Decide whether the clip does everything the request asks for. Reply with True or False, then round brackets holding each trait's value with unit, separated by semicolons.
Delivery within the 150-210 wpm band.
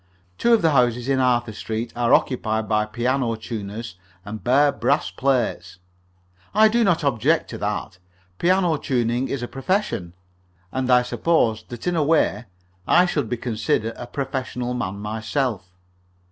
True (155 wpm)